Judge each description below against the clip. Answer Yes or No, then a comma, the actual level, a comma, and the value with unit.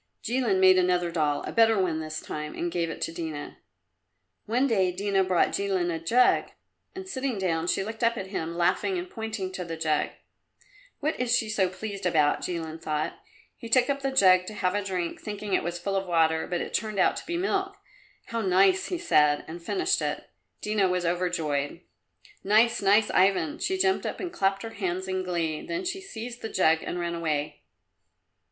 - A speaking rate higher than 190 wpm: Yes, average, 200 wpm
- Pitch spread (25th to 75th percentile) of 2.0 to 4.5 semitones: No, average, 5.0 semitones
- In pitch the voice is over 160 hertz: Yes, high, 190 Hz